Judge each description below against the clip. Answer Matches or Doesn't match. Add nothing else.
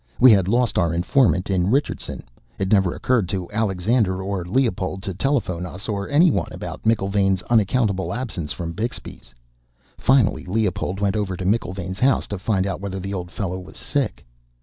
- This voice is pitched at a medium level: Doesn't match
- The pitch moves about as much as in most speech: Matches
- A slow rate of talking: Doesn't match